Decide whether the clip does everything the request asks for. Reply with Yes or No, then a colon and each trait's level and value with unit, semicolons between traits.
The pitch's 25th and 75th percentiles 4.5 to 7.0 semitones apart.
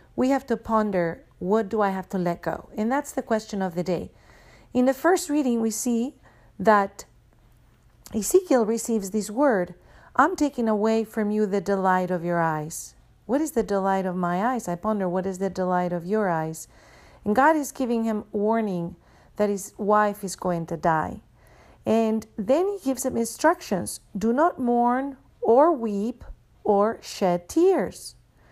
Yes: average, 4.9 semitones